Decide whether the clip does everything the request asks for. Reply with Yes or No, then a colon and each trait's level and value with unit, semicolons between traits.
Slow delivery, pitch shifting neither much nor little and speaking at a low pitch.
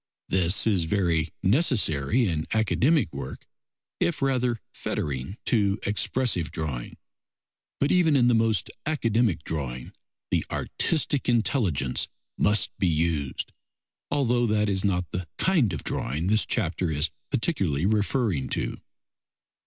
No: slow, 120 wpm; wide, 6.9 semitones; low, 100 Hz